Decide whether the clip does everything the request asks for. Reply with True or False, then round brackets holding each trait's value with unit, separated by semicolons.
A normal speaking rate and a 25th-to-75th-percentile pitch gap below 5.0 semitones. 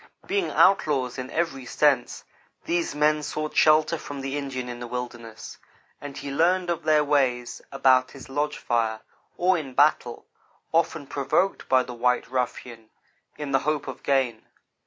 True (155 wpm; 3.5 semitones)